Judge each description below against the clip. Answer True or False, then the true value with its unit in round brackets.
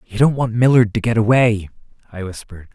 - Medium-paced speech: True (195 wpm)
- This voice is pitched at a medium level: False (110 Hz)